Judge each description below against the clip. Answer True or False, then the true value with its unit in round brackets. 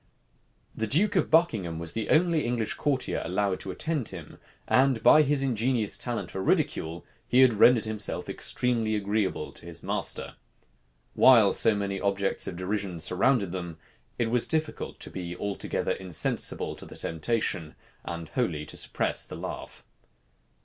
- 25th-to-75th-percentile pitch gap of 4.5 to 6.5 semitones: True (5.4 semitones)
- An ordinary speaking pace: True (155 wpm)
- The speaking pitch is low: True (105 Hz)